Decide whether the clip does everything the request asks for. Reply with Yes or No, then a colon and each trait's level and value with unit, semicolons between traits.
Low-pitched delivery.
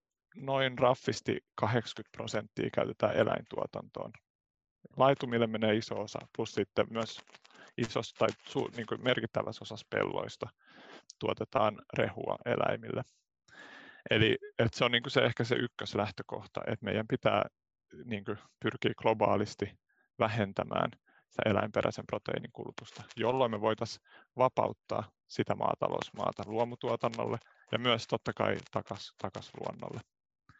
Yes: low, 115 Hz